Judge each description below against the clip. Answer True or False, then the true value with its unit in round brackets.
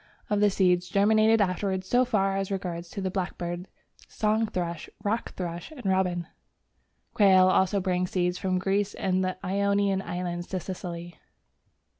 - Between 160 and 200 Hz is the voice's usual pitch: True (190 Hz)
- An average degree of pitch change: False (2.0 semitones)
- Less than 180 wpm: True (145 wpm)